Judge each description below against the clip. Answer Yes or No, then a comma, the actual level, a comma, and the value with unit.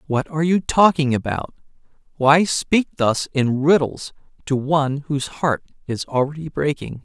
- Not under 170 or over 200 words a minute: No, slow, 135 wpm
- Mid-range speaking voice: Yes, medium, 145 Hz